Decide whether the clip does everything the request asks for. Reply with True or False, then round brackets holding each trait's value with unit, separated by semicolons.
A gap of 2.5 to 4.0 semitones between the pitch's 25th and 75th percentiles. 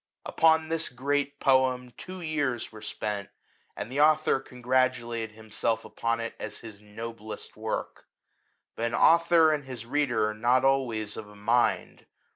False (4.4 semitones)